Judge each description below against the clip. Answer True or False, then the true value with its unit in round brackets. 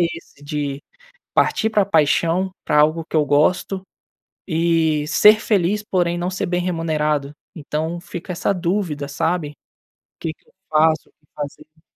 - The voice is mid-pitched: True (165 Hz)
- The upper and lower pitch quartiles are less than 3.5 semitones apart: True (3.0 semitones)